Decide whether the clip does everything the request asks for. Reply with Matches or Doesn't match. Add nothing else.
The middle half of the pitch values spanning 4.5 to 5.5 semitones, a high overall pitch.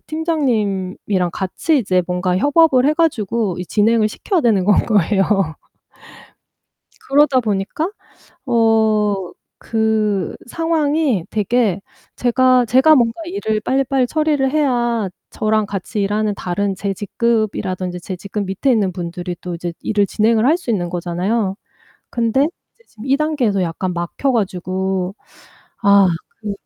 Matches